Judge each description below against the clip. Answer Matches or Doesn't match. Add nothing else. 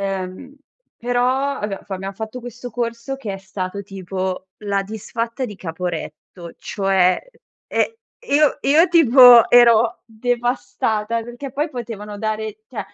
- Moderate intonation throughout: Matches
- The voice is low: Doesn't match